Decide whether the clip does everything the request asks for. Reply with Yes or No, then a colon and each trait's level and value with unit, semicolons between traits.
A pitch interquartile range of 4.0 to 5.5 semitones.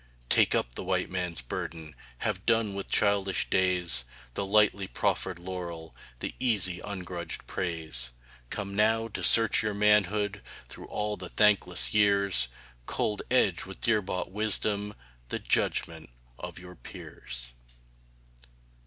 No: average, 3.0 semitones